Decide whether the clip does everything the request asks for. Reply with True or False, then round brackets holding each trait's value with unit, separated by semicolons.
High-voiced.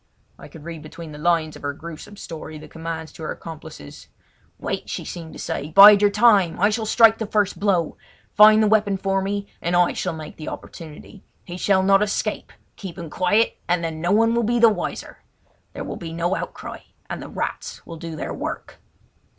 False (180 Hz)